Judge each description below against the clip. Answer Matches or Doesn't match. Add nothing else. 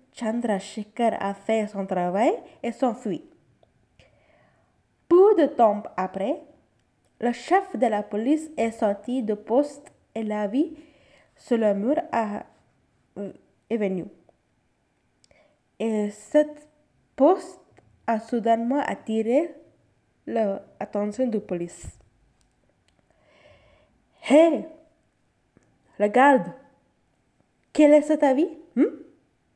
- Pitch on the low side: Doesn't match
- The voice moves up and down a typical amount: Doesn't match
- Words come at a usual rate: Doesn't match